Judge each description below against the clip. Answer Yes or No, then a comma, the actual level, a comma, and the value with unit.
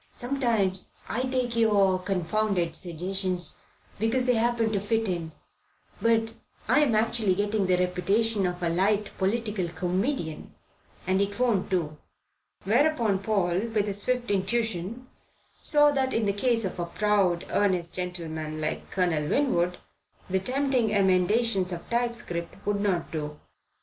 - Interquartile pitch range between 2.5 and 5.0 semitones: Yes, average, 4.2 semitones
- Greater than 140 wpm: No, slow, 135 wpm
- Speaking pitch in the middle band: No, high, 200 Hz